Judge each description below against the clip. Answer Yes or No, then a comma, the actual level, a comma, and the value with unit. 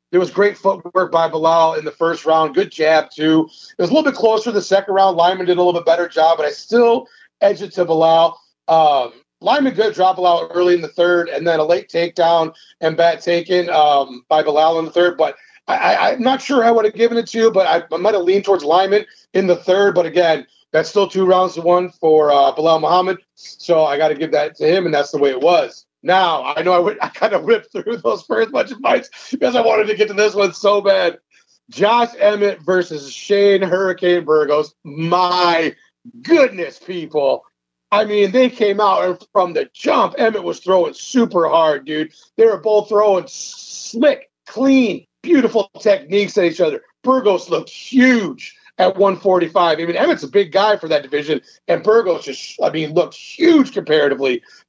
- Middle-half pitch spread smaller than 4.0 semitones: No, average, 4.7 semitones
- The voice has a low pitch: No, medium, 185 Hz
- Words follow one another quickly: Yes, fast, 210 wpm